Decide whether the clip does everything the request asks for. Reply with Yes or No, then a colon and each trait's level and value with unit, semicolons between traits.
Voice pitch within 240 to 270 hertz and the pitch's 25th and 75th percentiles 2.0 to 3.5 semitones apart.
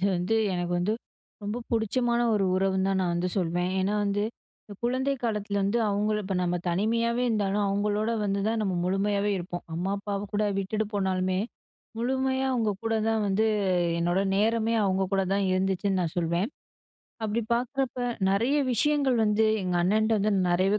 No: high, 205 Hz; average, 3.0 semitones